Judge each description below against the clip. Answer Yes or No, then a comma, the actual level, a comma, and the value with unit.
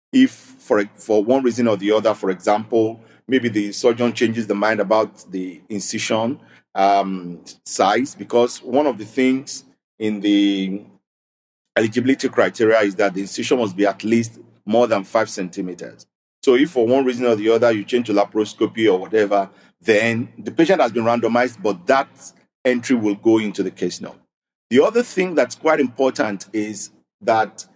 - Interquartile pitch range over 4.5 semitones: No, average, 3.4 semitones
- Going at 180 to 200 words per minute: No, average, 170 wpm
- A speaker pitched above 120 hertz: No, low, 110 Hz